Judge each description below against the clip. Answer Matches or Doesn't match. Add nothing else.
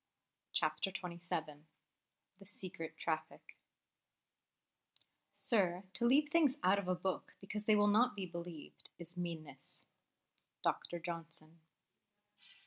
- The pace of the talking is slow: Matches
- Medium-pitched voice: Matches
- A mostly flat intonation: Doesn't match